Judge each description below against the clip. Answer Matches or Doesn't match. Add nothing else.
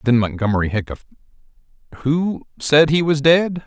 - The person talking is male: Matches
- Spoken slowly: Matches